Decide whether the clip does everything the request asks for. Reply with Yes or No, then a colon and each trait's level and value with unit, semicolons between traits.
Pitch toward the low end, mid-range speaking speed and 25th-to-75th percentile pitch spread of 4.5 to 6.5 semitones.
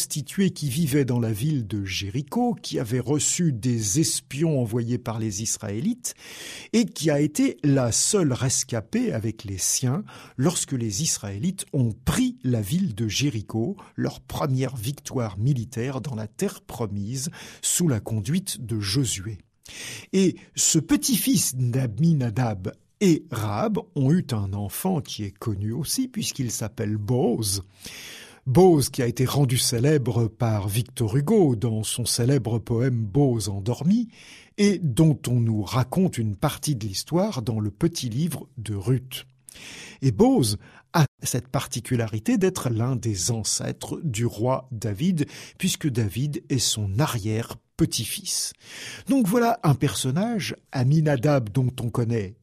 No: low, 130 Hz; slow, 140 wpm; average, 5.3 semitones